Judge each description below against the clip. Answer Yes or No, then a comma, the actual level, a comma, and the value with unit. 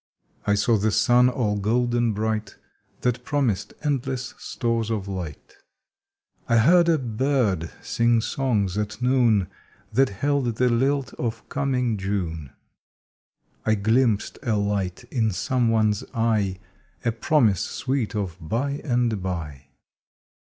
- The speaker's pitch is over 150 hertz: No, low, 115 Hz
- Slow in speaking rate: Yes, slow, 130 wpm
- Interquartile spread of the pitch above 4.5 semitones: No, average, 3.6 semitones